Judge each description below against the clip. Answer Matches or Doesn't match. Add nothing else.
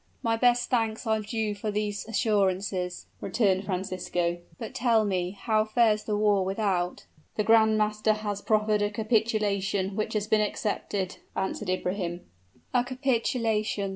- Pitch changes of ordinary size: Doesn't match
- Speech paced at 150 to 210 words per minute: Doesn't match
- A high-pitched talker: Matches